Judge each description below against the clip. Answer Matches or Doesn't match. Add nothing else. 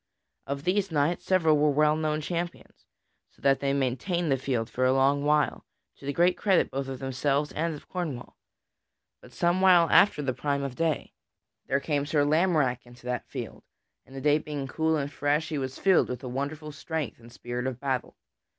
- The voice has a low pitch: Doesn't match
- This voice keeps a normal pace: Matches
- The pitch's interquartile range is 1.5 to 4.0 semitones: Matches